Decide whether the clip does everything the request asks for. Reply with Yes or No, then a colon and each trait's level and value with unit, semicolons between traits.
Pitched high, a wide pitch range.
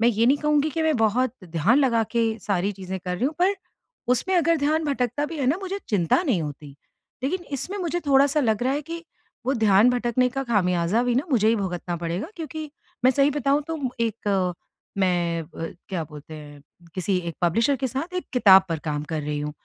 Yes: high, 235 Hz; wide, 8.1 semitones